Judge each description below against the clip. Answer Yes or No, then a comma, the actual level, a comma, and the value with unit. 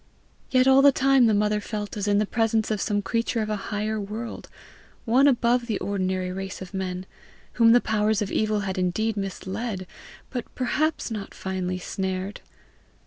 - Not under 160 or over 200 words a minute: Yes, average, 175 wpm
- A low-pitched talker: No, high, 210 Hz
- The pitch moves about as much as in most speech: Yes, average, 3.2 semitones